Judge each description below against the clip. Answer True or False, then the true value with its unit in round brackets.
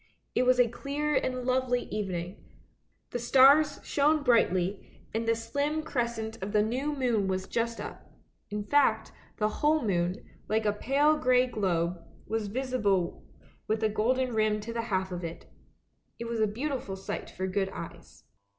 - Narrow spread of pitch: False (4.0 semitones)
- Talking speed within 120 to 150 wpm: False (165 wpm)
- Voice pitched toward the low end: False (230 Hz)